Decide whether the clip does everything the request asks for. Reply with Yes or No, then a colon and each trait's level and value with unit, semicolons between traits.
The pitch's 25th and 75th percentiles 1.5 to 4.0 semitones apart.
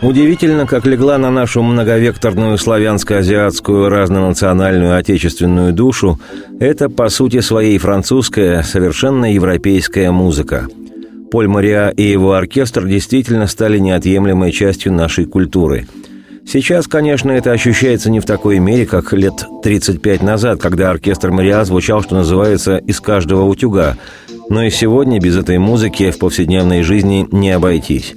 Yes: average, 3.7 semitones